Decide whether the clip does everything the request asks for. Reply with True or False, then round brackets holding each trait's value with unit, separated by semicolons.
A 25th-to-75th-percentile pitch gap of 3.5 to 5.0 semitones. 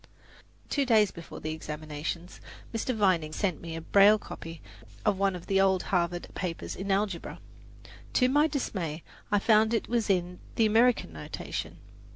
True (4.5 semitones)